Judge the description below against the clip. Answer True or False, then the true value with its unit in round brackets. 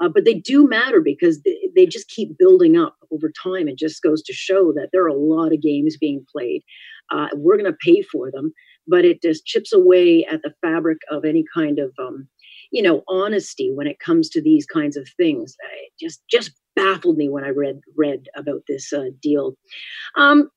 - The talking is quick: True (210 wpm)